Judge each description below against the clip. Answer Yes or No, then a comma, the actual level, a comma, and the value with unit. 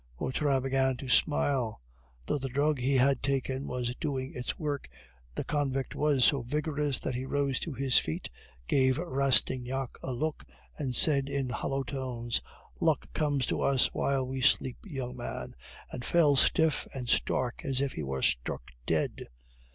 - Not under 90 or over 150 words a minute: No, average, 165 wpm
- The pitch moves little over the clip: Yes, narrow, 1.9 semitones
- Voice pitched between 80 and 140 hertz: Yes, low, 135 Hz